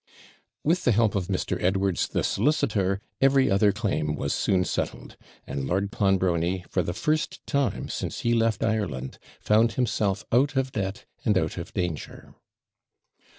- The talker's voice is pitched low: Yes, low, 100 Hz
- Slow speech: No, average, 150 wpm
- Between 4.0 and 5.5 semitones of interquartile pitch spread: Yes, average, 4.3 semitones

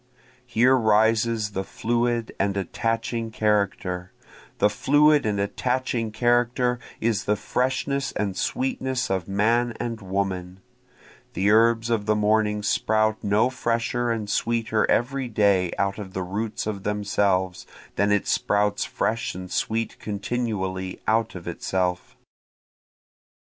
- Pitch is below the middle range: Yes, low, 110 Hz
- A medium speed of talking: No, slow, 125 wpm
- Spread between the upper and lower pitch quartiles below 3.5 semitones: Yes, average, 2.9 semitones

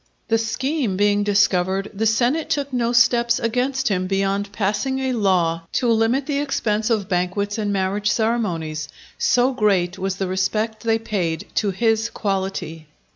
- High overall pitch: Yes, high, 210 Hz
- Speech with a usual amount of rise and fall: Yes, average, 3.7 semitones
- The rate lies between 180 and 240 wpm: No, average, 155 wpm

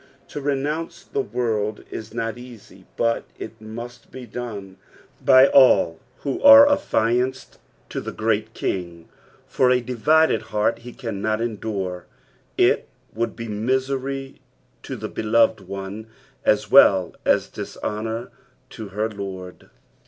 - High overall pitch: No, low, 115 Hz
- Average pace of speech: No, slow, 130 wpm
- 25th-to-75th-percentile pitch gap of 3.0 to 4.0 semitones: Yes, average, 3.5 semitones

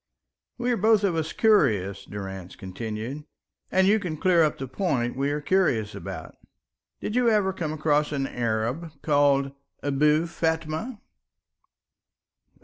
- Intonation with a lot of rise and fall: Yes, wide, 7.1 semitones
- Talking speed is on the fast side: No, average, 140 wpm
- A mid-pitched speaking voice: Yes, medium, 150 Hz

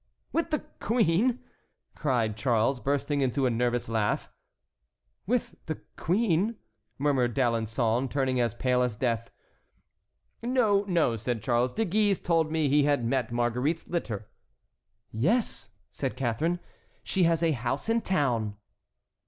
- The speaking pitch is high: No, low, 135 Hz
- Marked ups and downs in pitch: Yes, wide, 6.3 semitones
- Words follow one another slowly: Yes, slow, 130 wpm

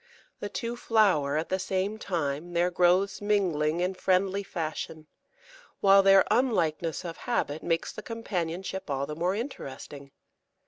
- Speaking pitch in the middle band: Yes, medium, 180 Hz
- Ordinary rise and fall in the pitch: Yes, average, 3.8 semitones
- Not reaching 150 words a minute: Yes, average, 140 wpm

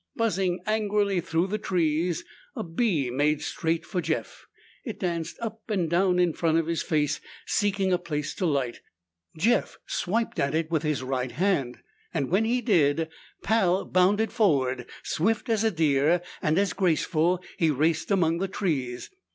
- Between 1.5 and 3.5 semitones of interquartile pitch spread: No, average, 4.4 semitones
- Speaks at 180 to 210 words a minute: No, average, 160 wpm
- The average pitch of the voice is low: No, medium, 170 Hz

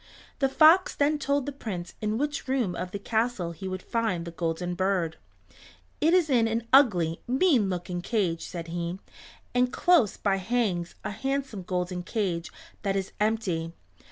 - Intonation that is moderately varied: No, wide, 6.1 semitones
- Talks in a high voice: Yes, high, 200 Hz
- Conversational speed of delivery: Yes, average, 165 wpm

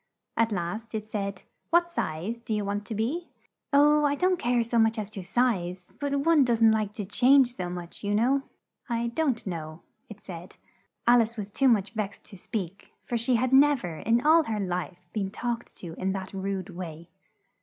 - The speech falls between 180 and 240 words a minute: Yes, average, 200 wpm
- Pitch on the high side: Yes, high, 220 Hz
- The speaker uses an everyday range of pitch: Yes, average, 4.3 semitones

